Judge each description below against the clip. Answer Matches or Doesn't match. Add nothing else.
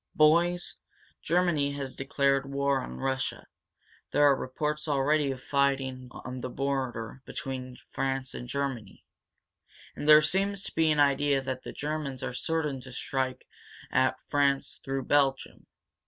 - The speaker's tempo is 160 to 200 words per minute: Doesn't match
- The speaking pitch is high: Doesn't match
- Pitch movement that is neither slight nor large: Doesn't match